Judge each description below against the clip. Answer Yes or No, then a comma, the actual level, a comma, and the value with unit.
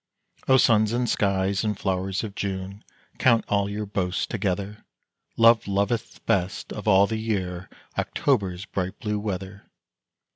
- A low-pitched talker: Yes, low, 100 Hz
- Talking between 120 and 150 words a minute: Yes, average, 140 wpm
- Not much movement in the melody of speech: Yes, narrow, 2.2 semitones